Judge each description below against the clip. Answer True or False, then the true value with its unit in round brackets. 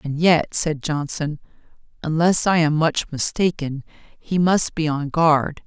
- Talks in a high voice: False (155 Hz)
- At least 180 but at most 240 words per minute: False (150 wpm)